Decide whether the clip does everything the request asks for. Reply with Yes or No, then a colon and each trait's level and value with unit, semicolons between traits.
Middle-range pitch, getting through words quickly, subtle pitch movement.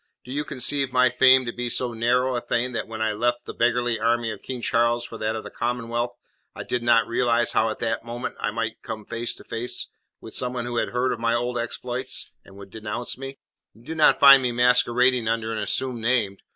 No: low, 120 Hz; fast, 230 wpm; narrow, 1.6 semitones